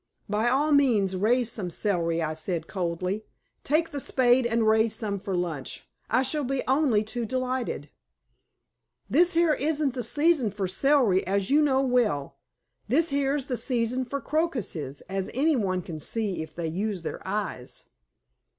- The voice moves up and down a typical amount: No, wide, 6.4 semitones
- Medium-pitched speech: No, high, 230 Hz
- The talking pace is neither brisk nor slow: Yes, average, 160 wpm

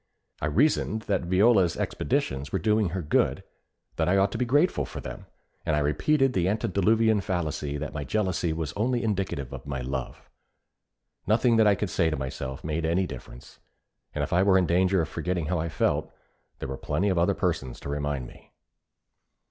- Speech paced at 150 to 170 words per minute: No, average, 190 wpm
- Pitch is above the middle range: No, very low, 90 Hz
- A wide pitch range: Yes, wide, 5.7 semitones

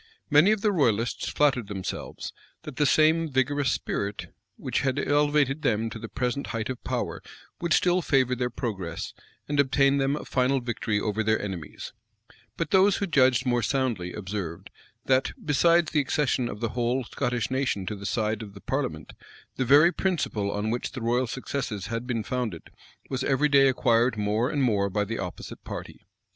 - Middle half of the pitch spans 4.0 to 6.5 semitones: Yes, average, 4.6 semitones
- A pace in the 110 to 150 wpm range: No, average, 180 wpm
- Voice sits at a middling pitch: No, low, 125 Hz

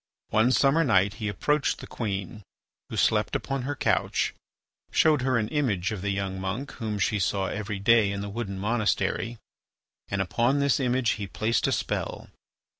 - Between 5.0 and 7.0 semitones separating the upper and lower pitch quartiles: No, average, 4.3 semitones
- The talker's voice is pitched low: Yes, low, 110 Hz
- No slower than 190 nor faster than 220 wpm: No, average, 175 wpm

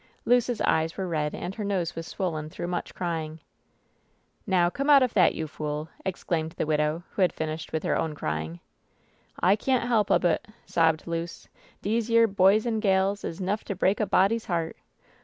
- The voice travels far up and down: No, average, 4.4 semitones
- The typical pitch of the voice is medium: Yes, medium, 180 Hz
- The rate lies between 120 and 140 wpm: No, average, 195 wpm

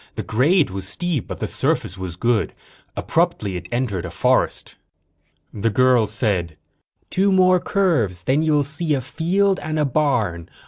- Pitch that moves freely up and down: Yes, wide, 8.5 semitones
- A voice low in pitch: Yes, low, 130 Hz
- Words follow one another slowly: No, average, 155 wpm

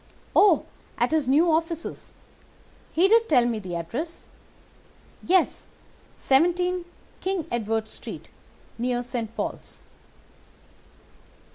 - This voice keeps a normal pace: No, slow, 100 wpm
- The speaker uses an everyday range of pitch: No, wide, 6.7 semitones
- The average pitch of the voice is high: Yes, very high, 310 Hz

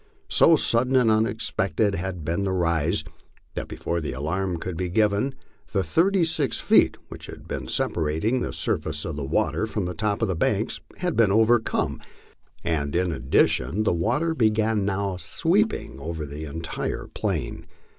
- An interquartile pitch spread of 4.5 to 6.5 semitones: Yes, average, 5.3 semitones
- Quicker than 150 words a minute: Yes, average, 160 wpm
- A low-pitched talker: Yes, very low, 95 Hz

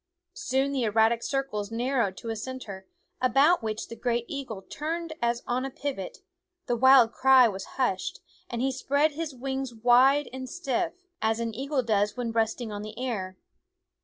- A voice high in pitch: Yes, high, 245 Hz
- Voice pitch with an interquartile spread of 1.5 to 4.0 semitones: Yes, average, 3.4 semitones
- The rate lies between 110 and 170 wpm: No, average, 185 wpm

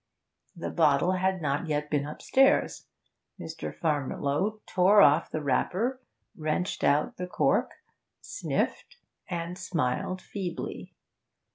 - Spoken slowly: Yes, slow, 110 wpm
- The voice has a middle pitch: Yes, medium, 170 Hz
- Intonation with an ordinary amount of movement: Yes, average, 4.0 semitones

